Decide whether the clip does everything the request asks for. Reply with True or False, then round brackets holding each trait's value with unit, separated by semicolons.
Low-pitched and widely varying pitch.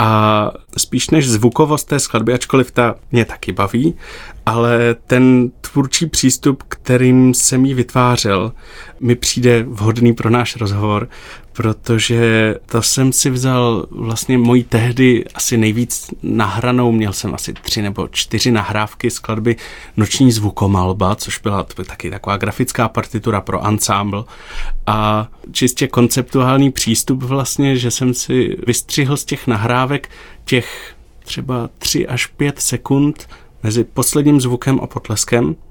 False (120 Hz; 2.8 semitones)